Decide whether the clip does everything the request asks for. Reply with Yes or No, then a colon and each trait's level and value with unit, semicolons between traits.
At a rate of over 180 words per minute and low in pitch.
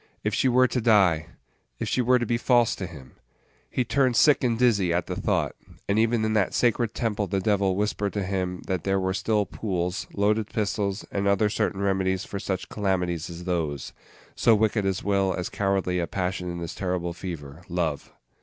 Yes: average, 200 wpm; low, 100 Hz